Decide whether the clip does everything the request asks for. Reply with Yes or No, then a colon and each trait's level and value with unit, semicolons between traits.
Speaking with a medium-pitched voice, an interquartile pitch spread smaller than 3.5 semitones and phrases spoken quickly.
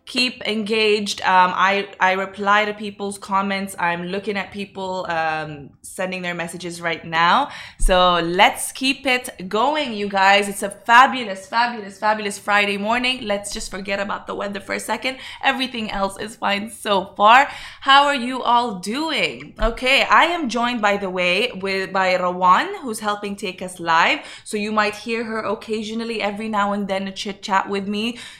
No: high, 205 Hz; average, 2.8 semitones; fast, 175 wpm